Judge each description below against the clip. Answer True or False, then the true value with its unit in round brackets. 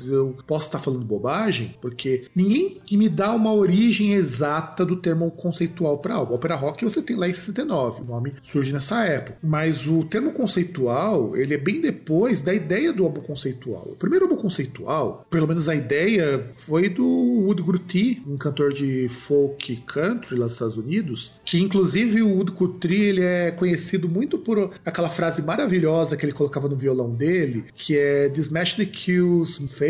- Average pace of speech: True (175 wpm)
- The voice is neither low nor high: True (165 Hz)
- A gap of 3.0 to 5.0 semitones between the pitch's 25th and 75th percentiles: False (5.4 semitones)